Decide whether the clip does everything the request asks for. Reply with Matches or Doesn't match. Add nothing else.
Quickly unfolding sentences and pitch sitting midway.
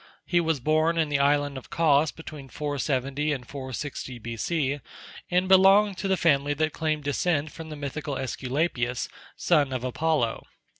Doesn't match